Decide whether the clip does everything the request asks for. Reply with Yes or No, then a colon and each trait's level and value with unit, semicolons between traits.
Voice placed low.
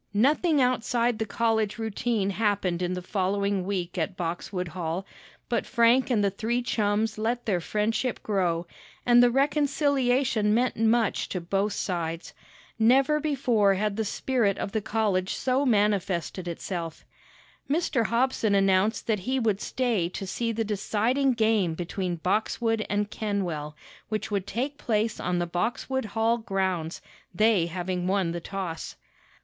No: high, 210 Hz